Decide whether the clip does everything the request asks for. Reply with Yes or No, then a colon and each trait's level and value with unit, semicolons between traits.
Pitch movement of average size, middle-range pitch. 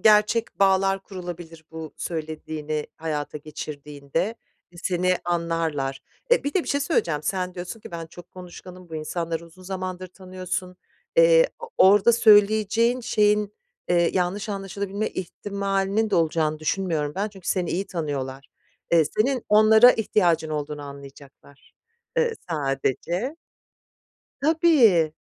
Yes: average, 4.7 semitones; medium, 180 Hz